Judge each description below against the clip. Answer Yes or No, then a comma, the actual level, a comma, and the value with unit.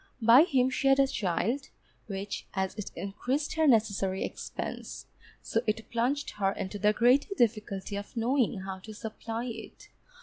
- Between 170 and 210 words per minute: No, average, 160 wpm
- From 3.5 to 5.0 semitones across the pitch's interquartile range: Yes, average, 4.2 semitones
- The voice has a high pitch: Yes, high, 225 Hz